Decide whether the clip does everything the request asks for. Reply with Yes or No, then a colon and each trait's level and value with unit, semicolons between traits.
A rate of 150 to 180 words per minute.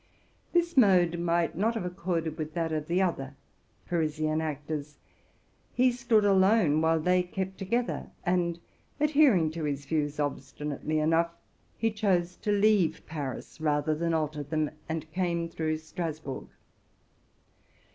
No: slow, 135 wpm